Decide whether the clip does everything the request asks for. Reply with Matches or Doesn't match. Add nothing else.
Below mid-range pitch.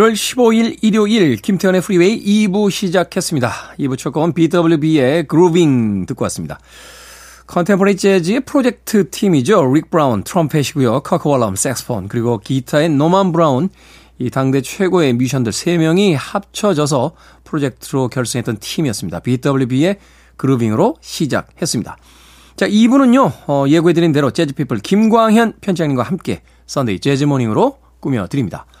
Doesn't match